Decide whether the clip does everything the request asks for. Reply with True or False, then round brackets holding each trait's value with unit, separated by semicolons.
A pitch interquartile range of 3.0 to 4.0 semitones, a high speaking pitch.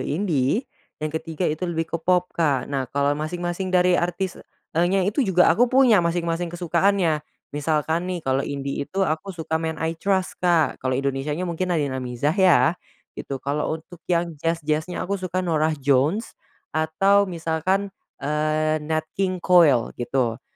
False (3.4 semitones; 165 Hz)